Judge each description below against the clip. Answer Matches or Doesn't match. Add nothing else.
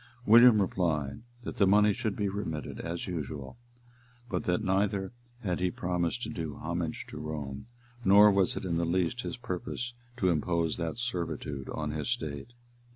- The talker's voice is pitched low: Matches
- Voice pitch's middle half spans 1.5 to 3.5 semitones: Doesn't match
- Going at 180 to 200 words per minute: Doesn't match